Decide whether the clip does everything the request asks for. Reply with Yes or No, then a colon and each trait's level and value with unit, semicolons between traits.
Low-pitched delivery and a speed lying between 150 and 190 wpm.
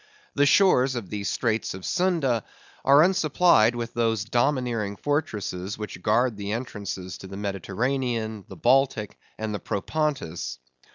No: low, 115 Hz; slow, 135 wpm